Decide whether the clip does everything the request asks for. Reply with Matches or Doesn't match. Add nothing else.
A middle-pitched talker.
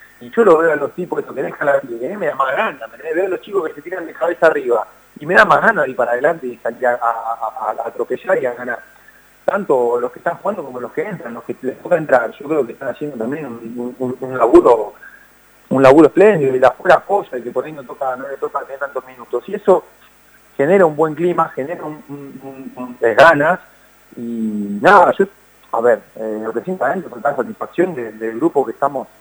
Doesn't match